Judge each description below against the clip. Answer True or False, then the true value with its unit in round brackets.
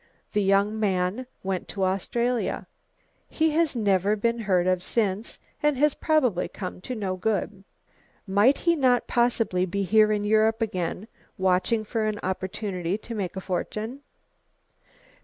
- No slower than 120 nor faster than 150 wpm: True (145 wpm)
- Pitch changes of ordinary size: True (3.7 semitones)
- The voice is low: False (210 Hz)